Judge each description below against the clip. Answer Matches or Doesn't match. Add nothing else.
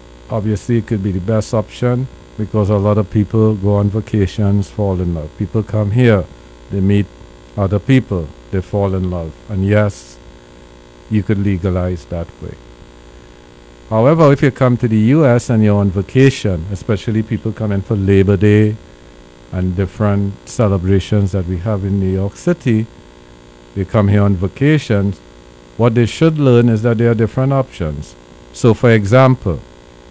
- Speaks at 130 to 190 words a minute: Matches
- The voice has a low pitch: Matches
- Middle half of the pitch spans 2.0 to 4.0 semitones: Doesn't match